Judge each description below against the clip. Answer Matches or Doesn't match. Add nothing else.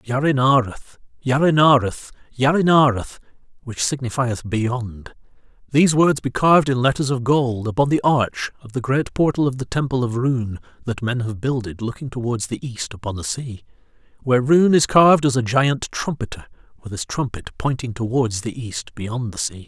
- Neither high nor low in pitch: Doesn't match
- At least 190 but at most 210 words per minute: Doesn't match